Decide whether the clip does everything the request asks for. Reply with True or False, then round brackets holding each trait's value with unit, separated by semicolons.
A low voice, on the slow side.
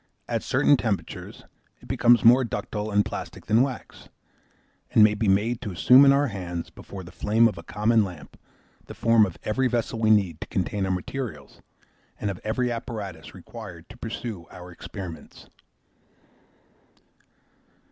False (105 Hz; 155 wpm)